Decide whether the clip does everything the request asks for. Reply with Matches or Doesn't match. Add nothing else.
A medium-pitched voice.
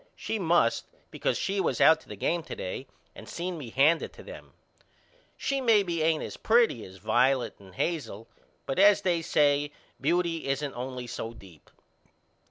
Matches